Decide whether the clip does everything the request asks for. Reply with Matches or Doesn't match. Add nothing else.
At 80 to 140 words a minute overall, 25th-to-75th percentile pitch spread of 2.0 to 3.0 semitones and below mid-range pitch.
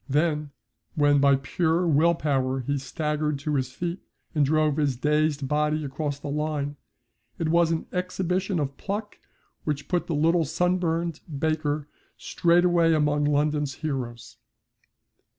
Doesn't match